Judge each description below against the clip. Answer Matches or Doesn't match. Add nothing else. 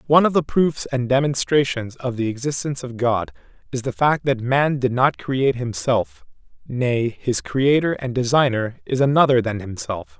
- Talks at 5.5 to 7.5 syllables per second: Doesn't match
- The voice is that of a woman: Doesn't match